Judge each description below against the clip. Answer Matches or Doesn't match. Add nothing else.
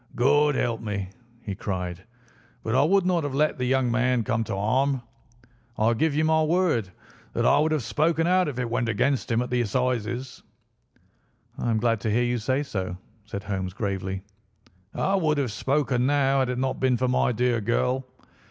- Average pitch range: Matches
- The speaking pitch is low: Matches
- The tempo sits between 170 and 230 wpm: Matches